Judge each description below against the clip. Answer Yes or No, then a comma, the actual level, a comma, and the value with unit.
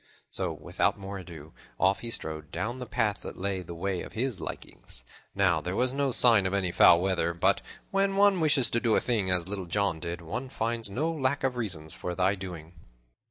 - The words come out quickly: Yes, fast, 210 wpm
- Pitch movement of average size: No, wide, 5.7 semitones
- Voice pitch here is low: Yes, low, 100 Hz